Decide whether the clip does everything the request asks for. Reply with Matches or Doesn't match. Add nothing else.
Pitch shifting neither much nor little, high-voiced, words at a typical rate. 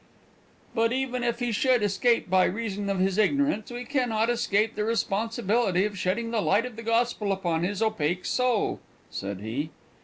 Matches